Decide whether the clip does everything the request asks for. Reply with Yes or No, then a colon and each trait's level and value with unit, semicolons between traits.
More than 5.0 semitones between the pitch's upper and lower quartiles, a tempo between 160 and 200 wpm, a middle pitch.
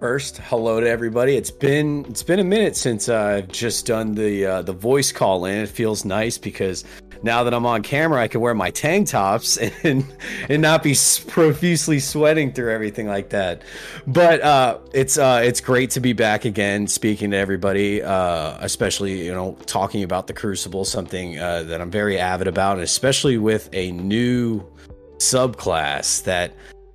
No: wide, 5.4 semitones; average, 180 wpm; low, 110 Hz